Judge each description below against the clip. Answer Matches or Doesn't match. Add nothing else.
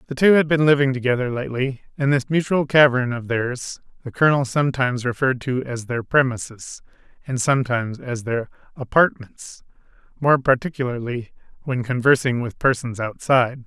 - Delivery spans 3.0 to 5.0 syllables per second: Doesn't match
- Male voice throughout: Matches